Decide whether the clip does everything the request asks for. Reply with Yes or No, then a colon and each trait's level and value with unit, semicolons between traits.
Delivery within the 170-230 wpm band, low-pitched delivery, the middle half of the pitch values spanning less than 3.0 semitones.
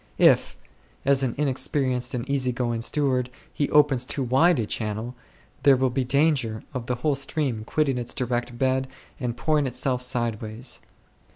No: average, 160 wpm; low, 130 Hz; narrow, 2.4 semitones